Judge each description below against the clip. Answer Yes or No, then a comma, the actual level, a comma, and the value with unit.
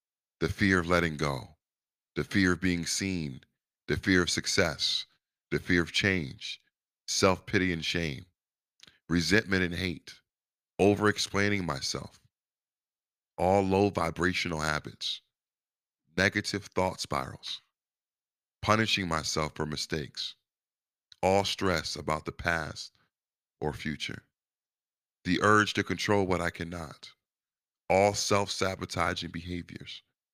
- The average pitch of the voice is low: Yes, very low, 90 Hz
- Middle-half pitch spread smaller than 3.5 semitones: Yes, average, 2.9 semitones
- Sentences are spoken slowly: Yes, slow, 115 wpm